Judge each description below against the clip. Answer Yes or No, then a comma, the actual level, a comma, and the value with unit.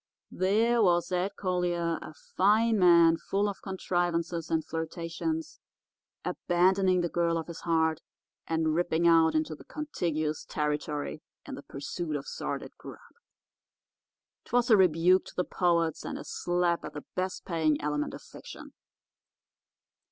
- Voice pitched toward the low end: No, medium, 170 Hz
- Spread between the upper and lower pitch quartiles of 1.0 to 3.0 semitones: Yes, narrow, 2.4 semitones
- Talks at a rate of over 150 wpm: No, average, 140 wpm